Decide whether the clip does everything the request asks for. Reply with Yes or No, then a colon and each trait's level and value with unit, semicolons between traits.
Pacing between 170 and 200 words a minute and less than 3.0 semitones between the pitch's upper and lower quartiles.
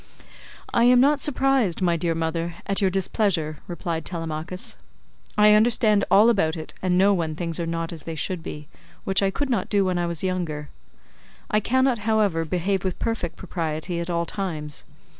No: average, 180 wpm; average, 4.1 semitones